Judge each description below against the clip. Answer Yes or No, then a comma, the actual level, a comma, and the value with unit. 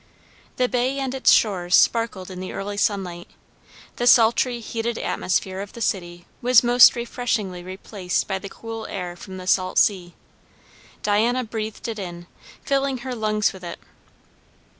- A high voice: Yes, high, 210 Hz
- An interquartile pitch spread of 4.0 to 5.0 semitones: Yes, average, 4.3 semitones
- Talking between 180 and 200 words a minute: No, average, 155 wpm